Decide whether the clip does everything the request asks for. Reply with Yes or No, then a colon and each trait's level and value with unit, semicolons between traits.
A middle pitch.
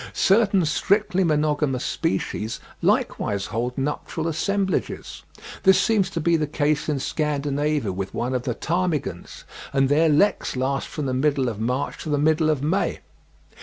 Yes: medium, 150 Hz